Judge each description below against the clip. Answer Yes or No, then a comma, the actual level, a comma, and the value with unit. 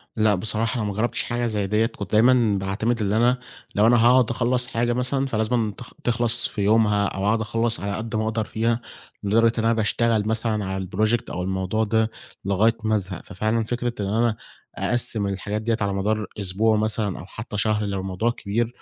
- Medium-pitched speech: No, low, 110 Hz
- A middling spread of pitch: No, narrow, 2.3 semitones